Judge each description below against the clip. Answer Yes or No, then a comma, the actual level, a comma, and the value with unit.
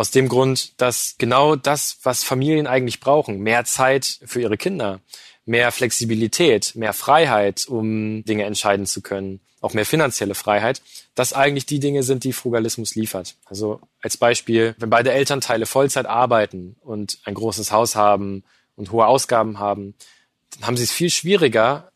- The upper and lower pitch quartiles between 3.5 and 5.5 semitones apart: Yes, average, 3.8 semitones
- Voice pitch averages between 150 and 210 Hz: No, low, 115 Hz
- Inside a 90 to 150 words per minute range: No, average, 160 wpm